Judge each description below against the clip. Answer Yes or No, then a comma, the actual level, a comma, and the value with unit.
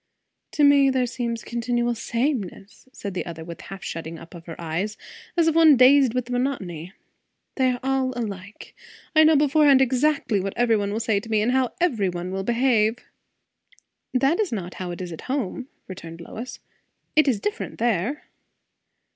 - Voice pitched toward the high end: Yes, high, 235 Hz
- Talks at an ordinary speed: Yes, average, 180 wpm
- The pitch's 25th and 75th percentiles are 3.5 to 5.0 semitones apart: No, wide, 5.6 semitones